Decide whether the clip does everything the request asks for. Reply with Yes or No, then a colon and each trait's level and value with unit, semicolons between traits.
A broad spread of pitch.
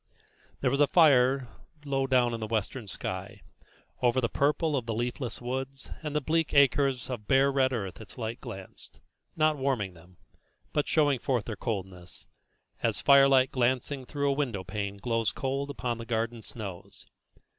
No: average, 3.5 semitones